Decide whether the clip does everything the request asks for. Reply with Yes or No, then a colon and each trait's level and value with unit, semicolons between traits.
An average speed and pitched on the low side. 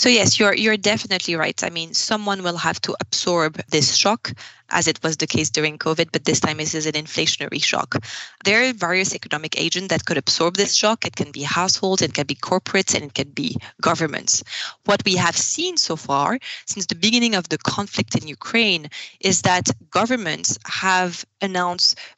No: average, 195 wpm; medium, 180 Hz